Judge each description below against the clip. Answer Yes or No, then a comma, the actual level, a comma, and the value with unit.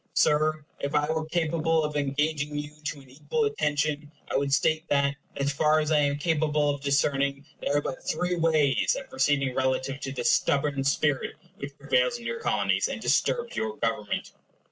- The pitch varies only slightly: Yes, narrow, 2.0 semitones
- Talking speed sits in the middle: Yes, average, 185 wpm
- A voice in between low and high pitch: Yes, medium, 150 Hz